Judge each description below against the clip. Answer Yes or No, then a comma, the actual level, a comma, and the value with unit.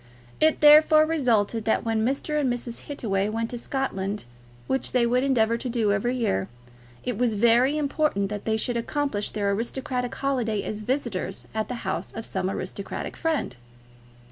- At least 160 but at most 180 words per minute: Yes, average, 170 wpm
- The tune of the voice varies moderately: Yes, average, 4.2 semitones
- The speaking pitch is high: Yes, high, 235 Hz